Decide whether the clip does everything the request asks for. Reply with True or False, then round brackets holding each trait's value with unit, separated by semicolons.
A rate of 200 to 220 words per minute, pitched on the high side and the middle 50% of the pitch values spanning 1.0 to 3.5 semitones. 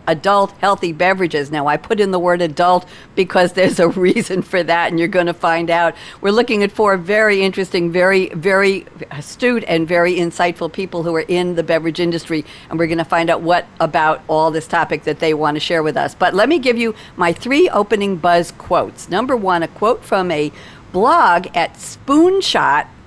False (205 wpm; 175 Hz; 2.8 semitones)